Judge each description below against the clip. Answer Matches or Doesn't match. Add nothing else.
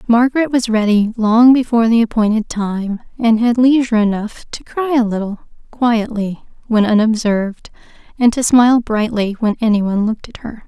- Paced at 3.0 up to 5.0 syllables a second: Doesn't match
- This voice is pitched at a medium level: Doesn't match